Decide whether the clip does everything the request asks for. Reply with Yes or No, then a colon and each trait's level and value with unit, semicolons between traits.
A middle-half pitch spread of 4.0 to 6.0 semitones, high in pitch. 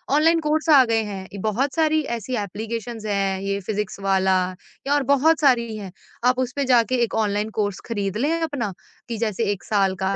Yes: average, 4.8 semitones; high, 220 Hz